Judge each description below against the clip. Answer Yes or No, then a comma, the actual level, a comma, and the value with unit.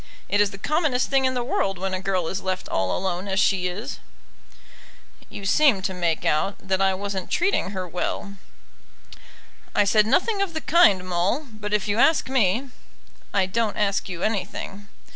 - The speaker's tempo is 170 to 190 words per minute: Yes, average, 185 wpm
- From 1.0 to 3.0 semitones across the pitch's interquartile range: No, average, 4.3 semitones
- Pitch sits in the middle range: No, high, 200 Hz